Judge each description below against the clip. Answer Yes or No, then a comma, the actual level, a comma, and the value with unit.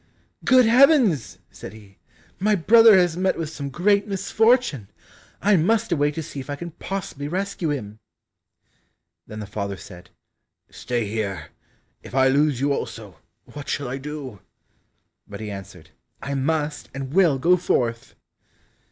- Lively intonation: Yes, wide, 8.3 semitones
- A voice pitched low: No, medium, 145 Hz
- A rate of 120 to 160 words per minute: Yes, average, 150 wpm